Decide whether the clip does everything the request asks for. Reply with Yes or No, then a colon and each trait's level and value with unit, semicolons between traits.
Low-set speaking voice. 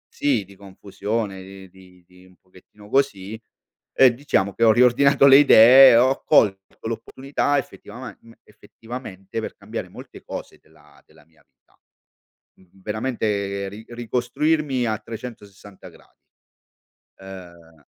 Yes: low, 110 Hz